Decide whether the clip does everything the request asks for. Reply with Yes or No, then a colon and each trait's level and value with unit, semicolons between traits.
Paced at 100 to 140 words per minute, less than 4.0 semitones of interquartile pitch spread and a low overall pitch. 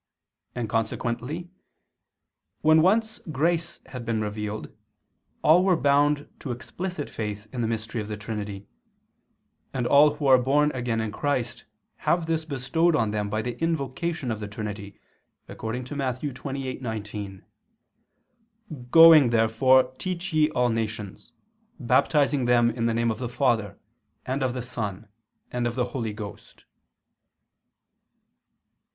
No: slow, 135 wpm; average, 4.8 semitones; low, 125 Hz